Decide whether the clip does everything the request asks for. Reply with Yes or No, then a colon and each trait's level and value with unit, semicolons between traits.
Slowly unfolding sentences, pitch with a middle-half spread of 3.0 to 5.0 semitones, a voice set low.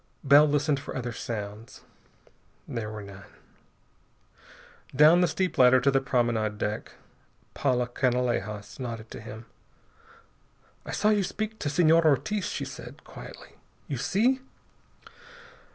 No: slow, 125 wpm; wide, 5.6 semitones; low, 130 Hz